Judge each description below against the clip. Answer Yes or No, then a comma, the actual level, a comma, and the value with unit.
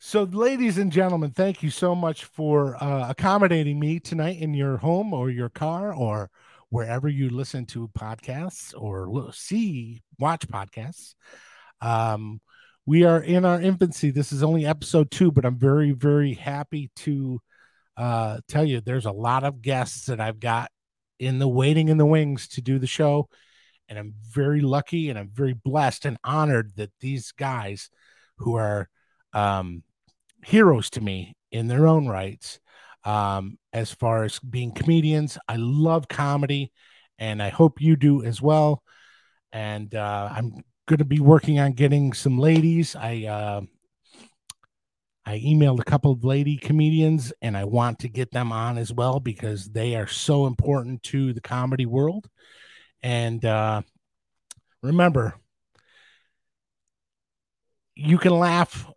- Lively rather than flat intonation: No, average, 5.0 semitones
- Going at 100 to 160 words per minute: Yes, average, 150 wpm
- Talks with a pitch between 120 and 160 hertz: Yes, low, 135 Hz